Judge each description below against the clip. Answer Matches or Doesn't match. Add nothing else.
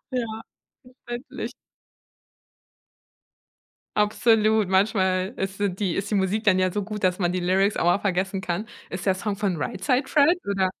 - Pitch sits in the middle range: Doesn't match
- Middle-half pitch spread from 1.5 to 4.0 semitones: Matches